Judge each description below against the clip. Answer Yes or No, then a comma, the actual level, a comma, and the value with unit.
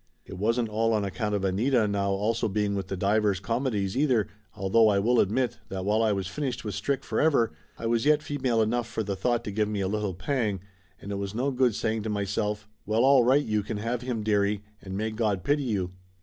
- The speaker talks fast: Yes, fast, 235 wpm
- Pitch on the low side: Yes, low, 110 Hz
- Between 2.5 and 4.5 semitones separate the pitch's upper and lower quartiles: Yes, average, 3.0 semitones